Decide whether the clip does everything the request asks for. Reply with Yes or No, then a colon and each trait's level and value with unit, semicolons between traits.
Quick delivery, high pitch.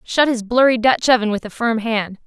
Yes: fast, 240 wpm; high, 230 Hz